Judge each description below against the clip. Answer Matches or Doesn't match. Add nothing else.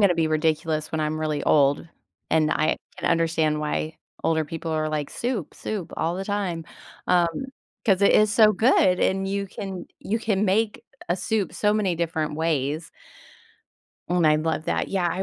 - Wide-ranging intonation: Doesn't match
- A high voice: Doesn't match